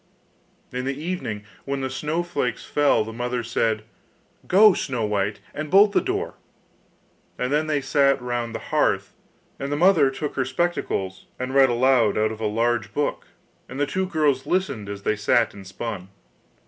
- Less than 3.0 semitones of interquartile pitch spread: No, average, 5.0 semitones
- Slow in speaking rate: No, average, 175 wpm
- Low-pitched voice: Yes, low, 130 Hz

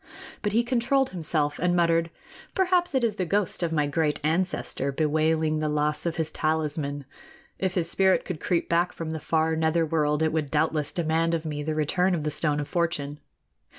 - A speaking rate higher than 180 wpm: Yes, average, 195 wpm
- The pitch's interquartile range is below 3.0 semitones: Yes, narrow, 2.6 semitones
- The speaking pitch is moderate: Yes, medium, 160 Hz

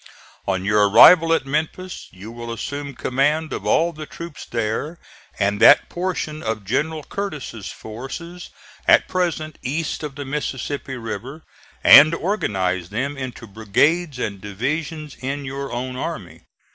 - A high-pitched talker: No, medium, 140 Hz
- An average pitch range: No, wide, 5.9 semitones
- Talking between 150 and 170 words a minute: No, average, 140 wpm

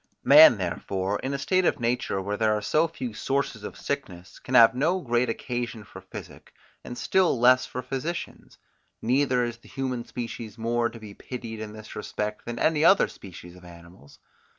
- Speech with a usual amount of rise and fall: Yes, average, 4.1 semitones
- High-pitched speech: No, low, 120 Hz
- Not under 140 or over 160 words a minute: No, average, 185 wpm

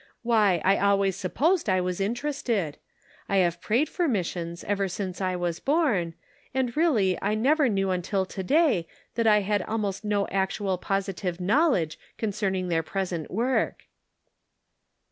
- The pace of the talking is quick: No, average, 145 wpm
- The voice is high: Yes, high, 195 Hz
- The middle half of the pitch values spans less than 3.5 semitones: No, average, 4.0 semitones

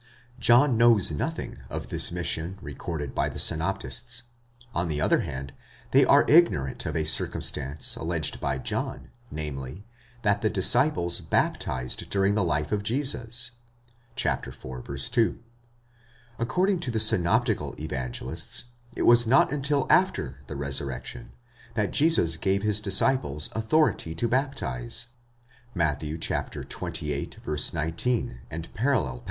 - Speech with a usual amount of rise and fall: No, wide, 8.3 semitones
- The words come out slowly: Yes, slow, 120 wpm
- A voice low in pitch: Yes, very low, 90 Hz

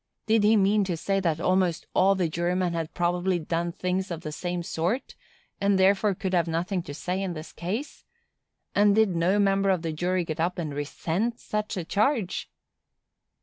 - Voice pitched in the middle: Yes, medium, 180 Hz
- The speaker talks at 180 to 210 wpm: Yes, average, 190 wpm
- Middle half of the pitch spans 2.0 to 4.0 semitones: Yes, average, 2.7 semitones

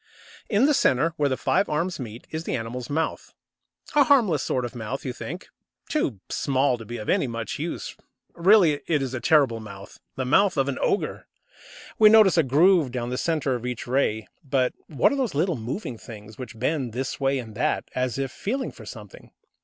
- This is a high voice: No, low, 135 Hz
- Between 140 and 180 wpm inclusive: No, average, 200 wpm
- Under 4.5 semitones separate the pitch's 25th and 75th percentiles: No, wide, 5.5 semitones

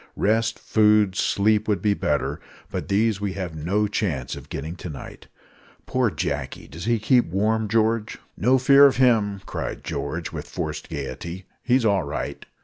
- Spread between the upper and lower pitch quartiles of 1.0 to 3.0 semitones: No, average, 4.2 semitones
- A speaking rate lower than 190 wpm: Yes, average, 165 wpm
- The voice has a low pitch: Yes, low, 105 Hz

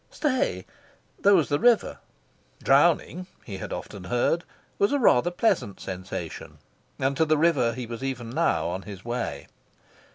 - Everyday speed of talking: Yes, average, 155 wpm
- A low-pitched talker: Yes, low, 125 Hz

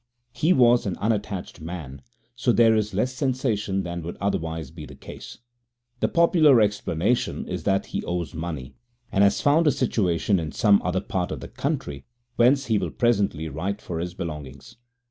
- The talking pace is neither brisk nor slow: Yes, average, 175 wpm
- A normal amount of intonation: No, wide, 6.0 semitones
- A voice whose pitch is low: Yes, low, 100 Hz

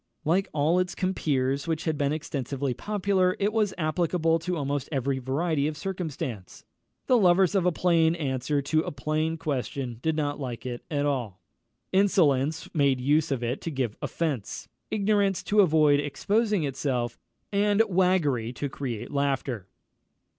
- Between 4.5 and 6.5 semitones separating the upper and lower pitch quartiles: Yes, average, 4.9 semitones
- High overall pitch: No, medium, 155 Hz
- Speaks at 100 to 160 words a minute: Yes, average, 155 wpm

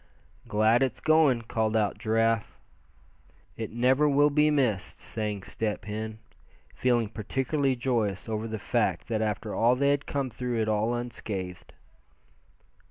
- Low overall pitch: Yes, low, 115 Hz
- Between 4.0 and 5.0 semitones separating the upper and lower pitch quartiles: No, average, 3.3 semitones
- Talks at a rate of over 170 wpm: No, average, 140 wpm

